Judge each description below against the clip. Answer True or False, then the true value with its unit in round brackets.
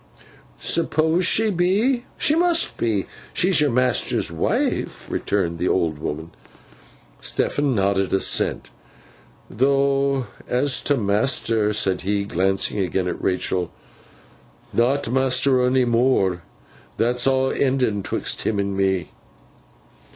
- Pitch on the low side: True (120 Hz)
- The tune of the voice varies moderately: False (6.2 semitones)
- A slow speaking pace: True (115 wpm)